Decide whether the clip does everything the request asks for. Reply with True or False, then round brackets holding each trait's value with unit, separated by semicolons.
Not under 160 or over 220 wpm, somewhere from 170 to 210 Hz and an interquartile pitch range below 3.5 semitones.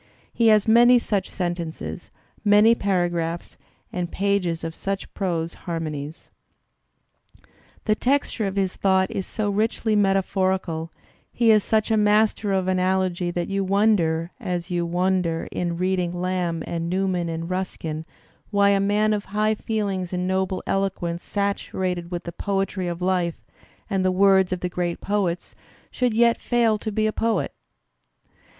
False (150 wpm; 190 Hz; 2.9 semitones)